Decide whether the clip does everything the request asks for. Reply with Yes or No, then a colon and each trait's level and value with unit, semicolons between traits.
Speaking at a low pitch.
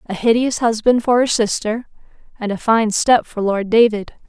No: high, 225 Hz